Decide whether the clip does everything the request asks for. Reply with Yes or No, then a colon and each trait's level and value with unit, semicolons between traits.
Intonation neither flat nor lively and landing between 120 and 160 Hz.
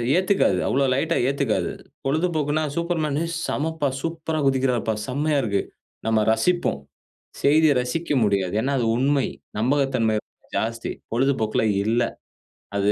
No: wide, 5.7 semitones; low, 135 Hz